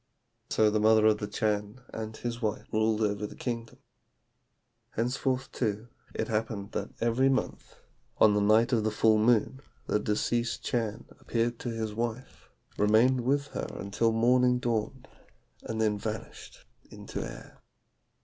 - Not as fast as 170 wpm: Yes, average, 150 wpm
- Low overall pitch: Yes, low, 110 Hz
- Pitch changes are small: Yes, narrow, 2.1 semitones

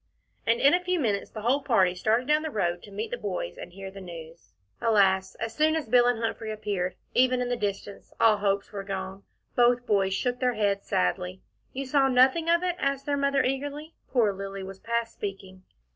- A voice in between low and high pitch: No, high, 220 Hz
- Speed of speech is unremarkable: No, fast, 210 wpm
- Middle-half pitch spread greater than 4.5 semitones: Yes, average, 5.0 semitones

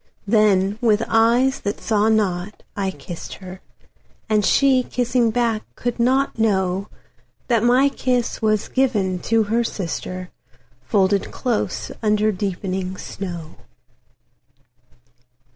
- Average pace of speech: No, slow, 100 wpm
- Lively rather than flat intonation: No, average, 3.8 semitones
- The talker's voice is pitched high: Yes, high, 215 Hz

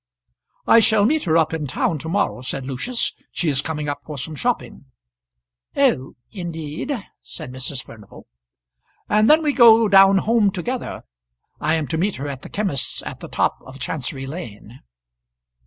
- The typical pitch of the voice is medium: Yes, medium, 160 Hz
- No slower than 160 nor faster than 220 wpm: Yes, average, 170 wpm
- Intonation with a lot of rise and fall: Yes, wide, 7.2 semitones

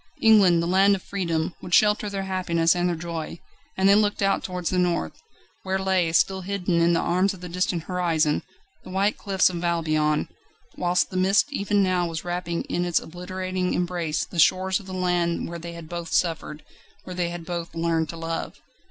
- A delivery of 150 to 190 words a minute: No, average, 200 wpm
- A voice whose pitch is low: No, medium, 180 Hz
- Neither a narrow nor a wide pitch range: No, narrow, 2.0 semitones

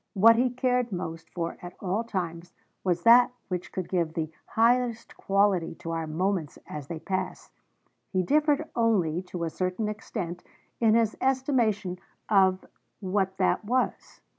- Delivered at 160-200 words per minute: No, average, 150 wpm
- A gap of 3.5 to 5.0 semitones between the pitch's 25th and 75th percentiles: Yes, average, 4.7 semitones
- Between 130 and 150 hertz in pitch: No, high, 190 Hz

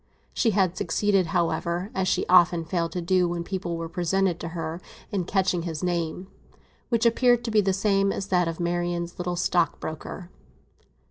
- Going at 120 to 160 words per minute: No, average, 175 wpm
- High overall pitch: No, medium, 180 Hz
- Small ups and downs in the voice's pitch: Yes, narrow, 2.1 semitones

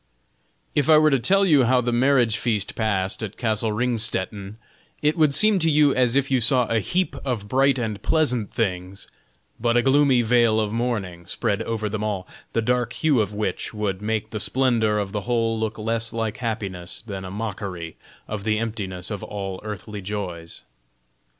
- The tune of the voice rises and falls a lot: No, average, 3.4 semitones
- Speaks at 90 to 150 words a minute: No, average, 185 wpm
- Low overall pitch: Yes, low, 110 Hz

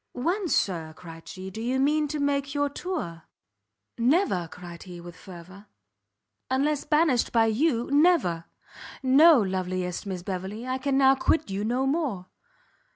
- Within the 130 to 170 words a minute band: Yes, average, 150 wpm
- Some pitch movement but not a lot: No, wide, 7.7 semitones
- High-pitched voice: Yes, high, 240 Hz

